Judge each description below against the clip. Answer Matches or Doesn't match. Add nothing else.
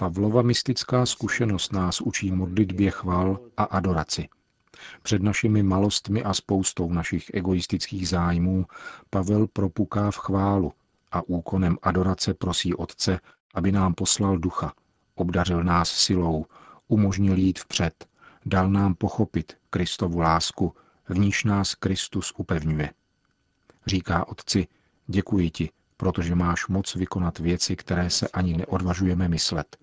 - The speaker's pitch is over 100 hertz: Doesn't match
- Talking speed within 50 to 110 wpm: Doesn't match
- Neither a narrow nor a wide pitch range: Doesn't match